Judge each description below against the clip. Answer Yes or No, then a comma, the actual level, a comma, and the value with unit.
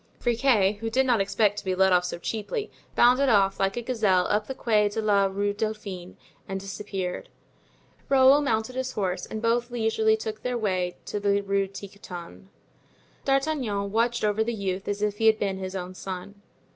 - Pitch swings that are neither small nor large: Yes, average, 3.0 semitones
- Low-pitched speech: No, high, 210 Hz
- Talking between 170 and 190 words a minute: Yes, average, 185 wpm